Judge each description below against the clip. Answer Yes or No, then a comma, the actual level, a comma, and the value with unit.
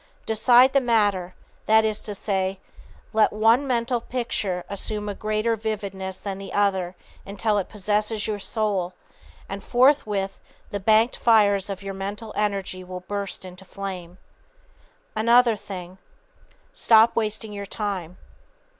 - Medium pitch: No, high, 205 Hz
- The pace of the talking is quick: No, slow, 135 wpm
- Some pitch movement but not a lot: No, narrow, 2.3 semitones